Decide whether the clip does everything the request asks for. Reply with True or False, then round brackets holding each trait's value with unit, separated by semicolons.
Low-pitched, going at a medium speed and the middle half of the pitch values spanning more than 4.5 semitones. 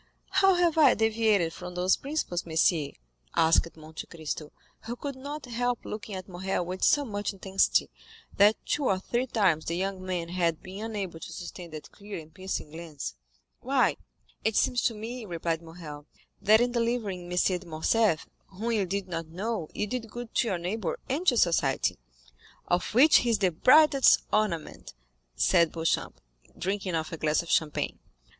False (190 Hz; 175 wpm; 5.3 semitones)